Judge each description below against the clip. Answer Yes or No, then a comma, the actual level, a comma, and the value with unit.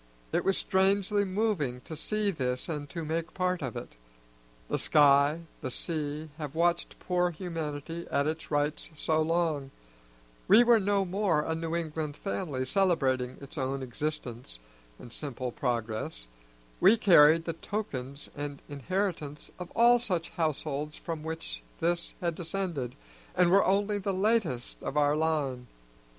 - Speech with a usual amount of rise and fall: Yes, average, 4.3 semitones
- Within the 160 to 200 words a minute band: No, average, 145 wpm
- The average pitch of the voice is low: No, medium, 160 Hz